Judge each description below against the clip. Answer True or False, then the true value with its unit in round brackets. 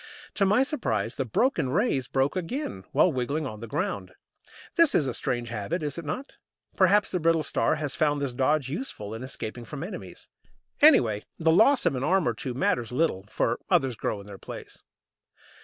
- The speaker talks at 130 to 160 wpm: False (190 wpm)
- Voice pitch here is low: False (145 Hz)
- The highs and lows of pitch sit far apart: True (7.2 semitones)